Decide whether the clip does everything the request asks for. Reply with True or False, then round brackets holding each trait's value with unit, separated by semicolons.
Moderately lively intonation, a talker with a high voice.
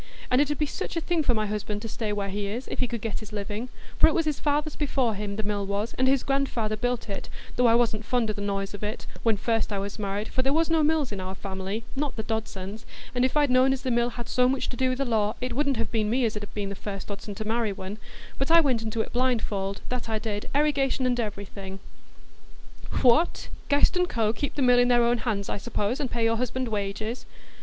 True (3.8 semitones; 230 Hz)